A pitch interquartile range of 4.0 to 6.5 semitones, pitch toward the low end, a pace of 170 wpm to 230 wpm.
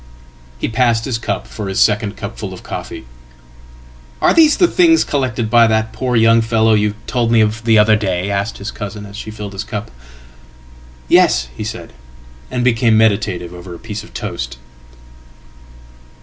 No: average, 5.0 semitones; low, 105 Hz; average, 160 wpm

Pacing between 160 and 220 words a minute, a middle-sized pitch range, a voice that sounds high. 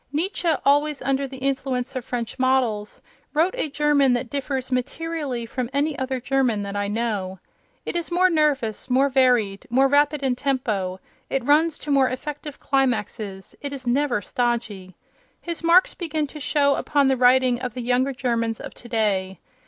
Yes: average, 170 wpm; average, 3.3 semitones; very high, 260 Hz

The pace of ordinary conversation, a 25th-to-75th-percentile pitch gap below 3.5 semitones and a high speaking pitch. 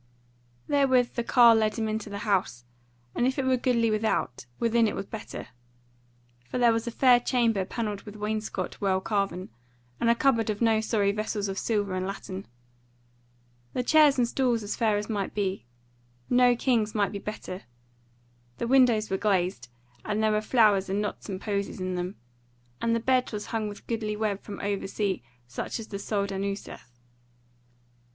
Yes: average, 180 wpm; average, 2.8 semitones; high, 215 Hz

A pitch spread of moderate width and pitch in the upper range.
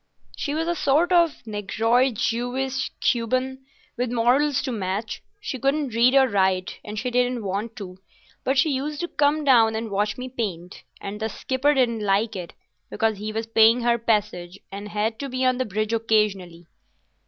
Yes: average, 3.8 semitones; high, 230 Hz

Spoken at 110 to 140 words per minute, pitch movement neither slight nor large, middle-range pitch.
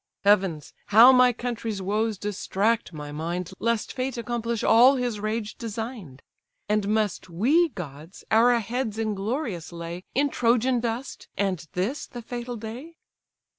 No: slow, 135 wpm; average, 3.9 semitones; high, 220 Hz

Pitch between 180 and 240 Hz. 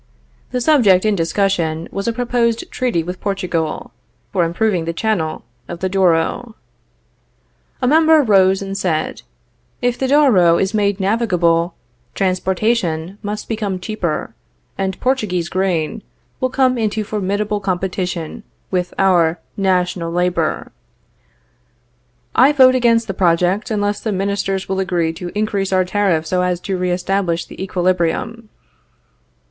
Yes: high, 190 Hz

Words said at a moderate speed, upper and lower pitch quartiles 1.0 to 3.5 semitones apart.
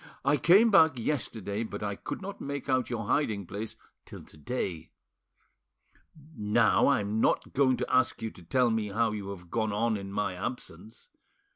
No: average, 175 wpm; average, 4.2 semitones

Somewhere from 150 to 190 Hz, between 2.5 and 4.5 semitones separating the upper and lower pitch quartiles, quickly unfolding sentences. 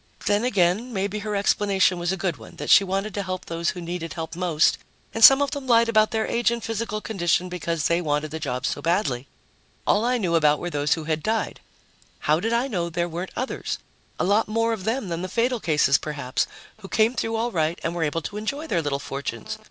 No: medium, 185 Hz; average, 5.2 semitones; fast, 230 wpm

